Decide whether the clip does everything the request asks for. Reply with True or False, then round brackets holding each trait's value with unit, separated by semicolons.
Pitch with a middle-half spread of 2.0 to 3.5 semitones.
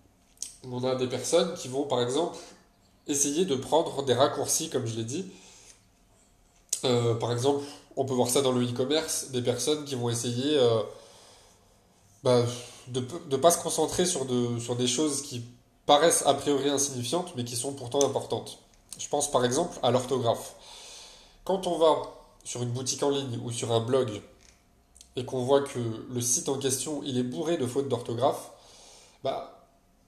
True (2.8 semitones)